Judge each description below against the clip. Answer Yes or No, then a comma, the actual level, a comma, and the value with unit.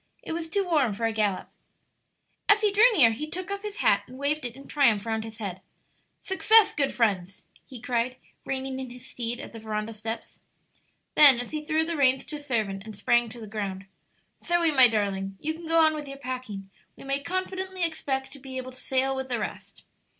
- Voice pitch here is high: Yes, very high, 260 Hz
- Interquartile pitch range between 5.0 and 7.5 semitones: Yes, wide, 5.6 semitones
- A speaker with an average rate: No, fast, 215 wpm